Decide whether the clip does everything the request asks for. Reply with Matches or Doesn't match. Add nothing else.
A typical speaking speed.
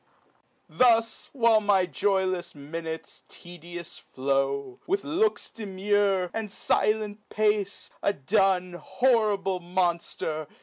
Doesn't match